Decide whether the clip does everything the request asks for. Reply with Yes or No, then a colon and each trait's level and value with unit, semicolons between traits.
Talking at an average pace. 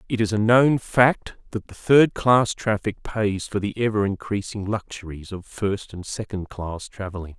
Yes: average, 180 wpm